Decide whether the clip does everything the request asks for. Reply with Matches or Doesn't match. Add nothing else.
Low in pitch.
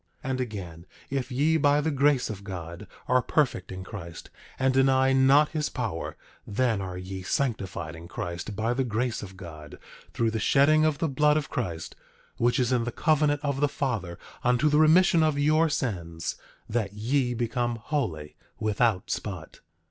Matches